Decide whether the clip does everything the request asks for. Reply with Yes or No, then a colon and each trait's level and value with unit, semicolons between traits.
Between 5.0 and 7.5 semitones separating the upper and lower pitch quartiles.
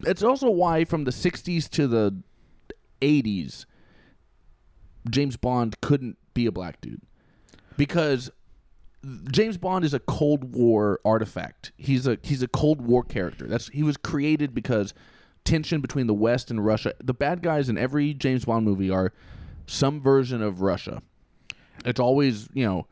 Yes: average, 5.3 semitones